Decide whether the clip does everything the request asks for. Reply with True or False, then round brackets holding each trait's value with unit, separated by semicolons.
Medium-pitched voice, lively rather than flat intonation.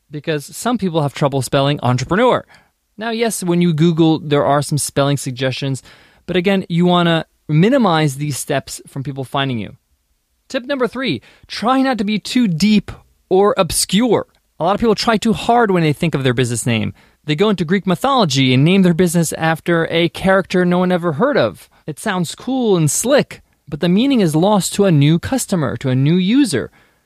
True (175 Hz; 6.3 semitones)